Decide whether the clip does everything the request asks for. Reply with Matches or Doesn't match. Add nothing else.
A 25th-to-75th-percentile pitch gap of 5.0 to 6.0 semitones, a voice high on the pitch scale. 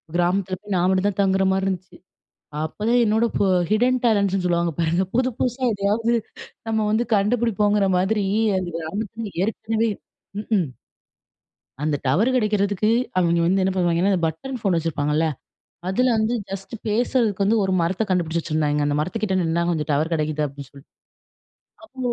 Doesn't match